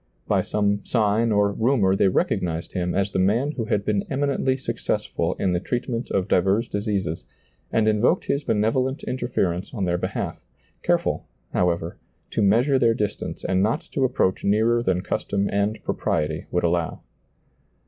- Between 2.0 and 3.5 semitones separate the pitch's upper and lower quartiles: No, average, 4.0 semitones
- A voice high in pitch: No, low, 105 Hz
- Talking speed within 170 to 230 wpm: No, average, 160 wpm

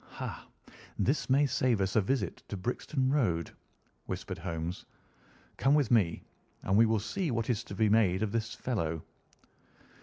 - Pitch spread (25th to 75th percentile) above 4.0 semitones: Yes, average, 5.3 semitones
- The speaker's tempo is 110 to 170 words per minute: Yes, average, 160 wpm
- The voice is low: Yes, low, 110 Hz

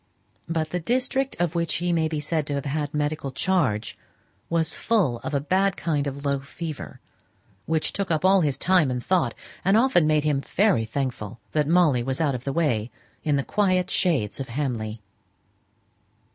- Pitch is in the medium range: Yes, medium, 155 Hz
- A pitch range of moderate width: Yes, average, 4.3 semitones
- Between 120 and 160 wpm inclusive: No, average, 185 wpm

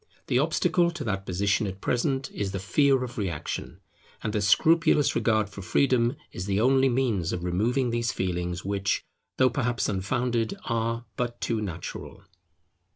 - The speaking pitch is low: Yes, low, 115 Hz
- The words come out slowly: No, average, 155 wpm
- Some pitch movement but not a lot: Yes, average, 4.4 semitones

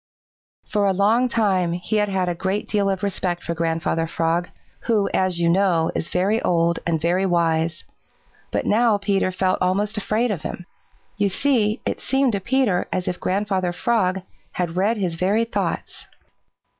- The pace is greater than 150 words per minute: Yes, average, 170 wpm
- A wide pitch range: No, average, 3.1 semitones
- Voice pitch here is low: No, high, 190 Hz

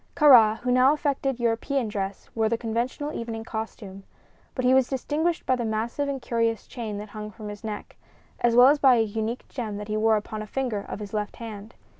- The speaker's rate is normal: No, fast, 215 wpm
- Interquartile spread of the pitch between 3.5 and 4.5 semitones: No, average, 3.1 semitones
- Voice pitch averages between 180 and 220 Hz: No, high, 230 Hz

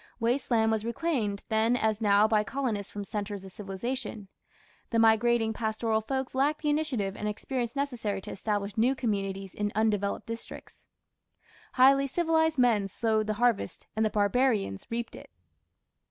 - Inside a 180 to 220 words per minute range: No, average, 155 wpm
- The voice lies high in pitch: Yes, high, 220 Hz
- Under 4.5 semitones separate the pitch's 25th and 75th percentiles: Yes, average, 3.3 semitones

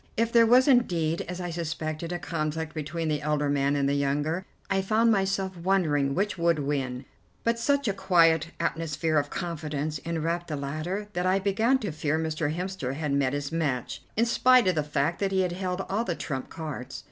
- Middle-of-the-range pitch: Yes, medium, 165 Hz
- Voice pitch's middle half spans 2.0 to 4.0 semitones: No, average, 4.4 semitones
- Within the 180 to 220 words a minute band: Yes, average, 195 wpm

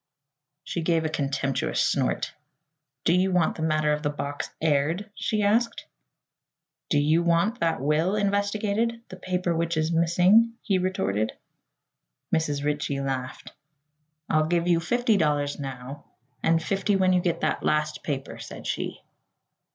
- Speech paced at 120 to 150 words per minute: Yes, average, 145 wpm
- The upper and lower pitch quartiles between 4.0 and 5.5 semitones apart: Yes, average, 4.3 semitones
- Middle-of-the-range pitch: Yes, medium, 165 Hz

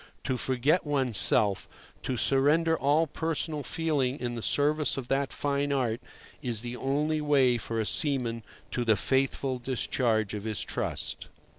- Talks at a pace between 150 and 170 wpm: Yes, average, 155 wpm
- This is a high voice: No, low, 135 Hz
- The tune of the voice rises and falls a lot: No, average, 3.5 semitones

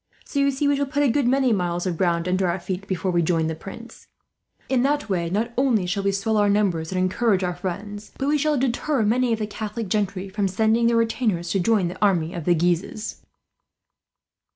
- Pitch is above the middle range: Yes, high, 205 Hz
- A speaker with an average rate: No, fast, 225 wpm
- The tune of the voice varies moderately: Yes, average, 4.6 semitones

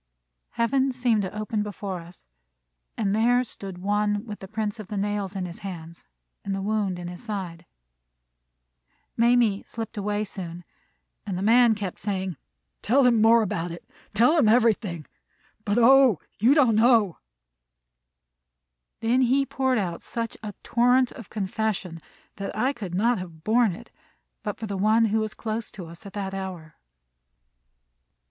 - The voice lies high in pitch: Yes, high, 210 Hz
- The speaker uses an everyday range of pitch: Yes, average, 3.5 semitones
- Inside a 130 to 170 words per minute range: Yes, average, 155 wpm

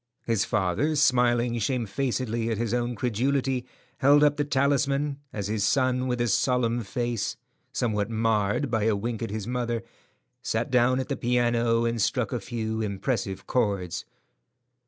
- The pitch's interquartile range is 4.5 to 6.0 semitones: No, narrow, 2.5 semitones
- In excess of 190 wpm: No, average, 155 wpm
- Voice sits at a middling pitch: No, low, 120 Hz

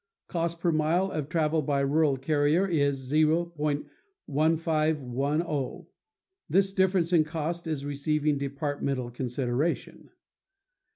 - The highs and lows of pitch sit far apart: No, average, 2.8 semitones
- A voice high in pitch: No, medium, 155 Hz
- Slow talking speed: Yes, slow, 100 wpm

